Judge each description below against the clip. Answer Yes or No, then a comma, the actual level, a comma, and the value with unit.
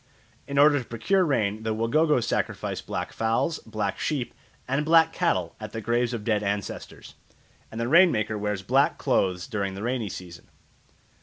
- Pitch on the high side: No, low, 115 Hz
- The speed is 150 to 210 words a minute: Yes, average, 170 wpm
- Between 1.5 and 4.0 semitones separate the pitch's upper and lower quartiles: No, average, 5.2 semitones